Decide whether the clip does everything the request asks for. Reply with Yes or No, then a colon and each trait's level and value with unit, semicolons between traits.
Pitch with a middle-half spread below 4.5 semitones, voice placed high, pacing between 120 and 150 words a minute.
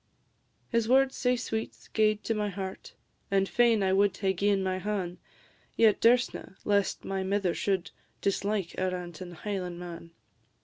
Yes: narrow, 2.4 semitones; high, 200 Hz; average, 145 wpm